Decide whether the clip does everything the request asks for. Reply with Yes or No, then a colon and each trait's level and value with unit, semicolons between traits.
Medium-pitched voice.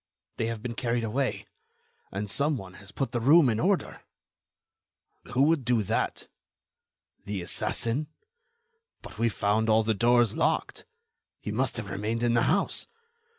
No: low, 115 Hz